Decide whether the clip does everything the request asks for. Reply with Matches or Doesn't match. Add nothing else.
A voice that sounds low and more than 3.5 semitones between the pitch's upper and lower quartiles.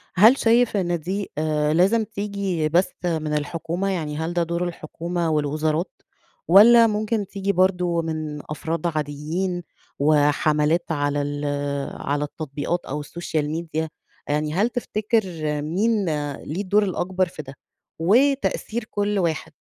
Doesn't match